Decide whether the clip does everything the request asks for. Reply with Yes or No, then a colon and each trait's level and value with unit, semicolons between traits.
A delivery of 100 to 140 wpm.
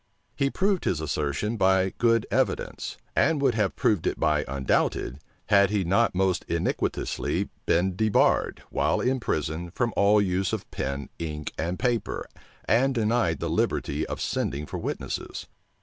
No: average, 150 wpm